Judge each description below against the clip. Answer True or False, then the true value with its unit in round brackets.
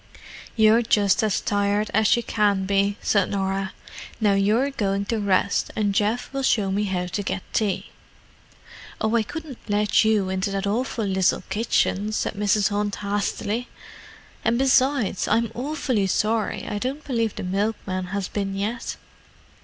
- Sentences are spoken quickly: False (150 wpm)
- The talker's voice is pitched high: True (210 Hz)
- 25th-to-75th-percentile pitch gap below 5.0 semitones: True (2.5 semitones)